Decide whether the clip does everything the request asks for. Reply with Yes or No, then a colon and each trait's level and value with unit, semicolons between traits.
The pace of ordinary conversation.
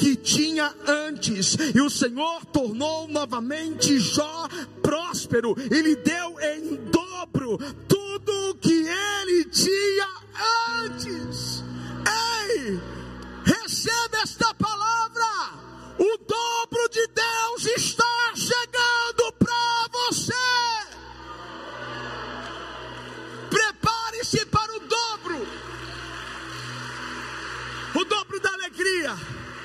No: slow, 85 wpm